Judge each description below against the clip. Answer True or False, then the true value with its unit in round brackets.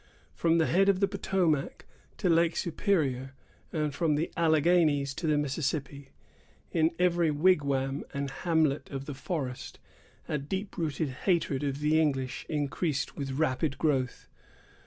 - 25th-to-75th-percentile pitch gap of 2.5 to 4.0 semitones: True (3.3 semitones)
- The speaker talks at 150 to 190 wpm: False (140 wpm)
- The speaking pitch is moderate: True (150 Hz)